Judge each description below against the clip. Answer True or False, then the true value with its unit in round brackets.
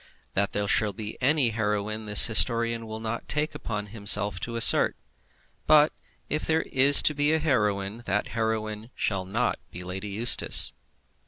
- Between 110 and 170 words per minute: True (150 wpm)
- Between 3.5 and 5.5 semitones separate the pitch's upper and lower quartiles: False (2.5 semitones)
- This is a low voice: True (110 Hz)